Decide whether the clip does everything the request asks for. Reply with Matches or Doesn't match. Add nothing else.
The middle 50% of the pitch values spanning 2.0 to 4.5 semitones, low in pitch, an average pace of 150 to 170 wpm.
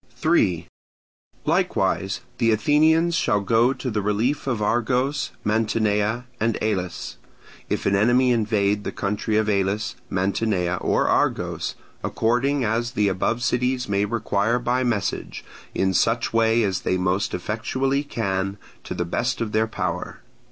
Doesn't match